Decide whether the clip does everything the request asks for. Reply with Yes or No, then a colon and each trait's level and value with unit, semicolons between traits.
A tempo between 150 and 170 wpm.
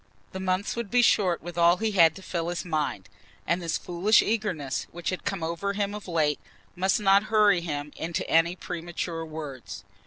No: average, 190 wpm